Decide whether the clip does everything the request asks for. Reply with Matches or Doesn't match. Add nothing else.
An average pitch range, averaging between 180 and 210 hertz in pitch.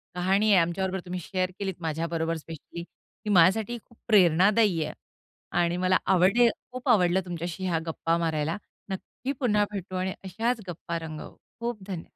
Matches